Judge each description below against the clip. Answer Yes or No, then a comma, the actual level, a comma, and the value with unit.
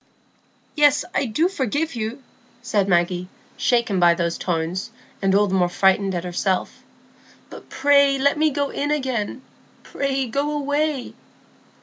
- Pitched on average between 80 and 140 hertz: No, high, 245 Hz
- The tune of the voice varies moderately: No, wide, 7.0 semitones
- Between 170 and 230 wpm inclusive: No, average, 140 wpm